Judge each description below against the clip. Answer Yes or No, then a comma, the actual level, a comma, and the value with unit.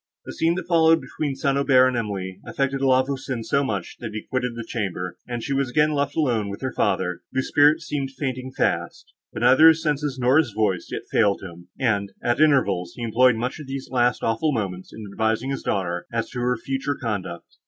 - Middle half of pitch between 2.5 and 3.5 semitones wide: No, average, 4.4 semitones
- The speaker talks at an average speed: No, fast, 215 wpm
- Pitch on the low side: Yes, low, 125 Hz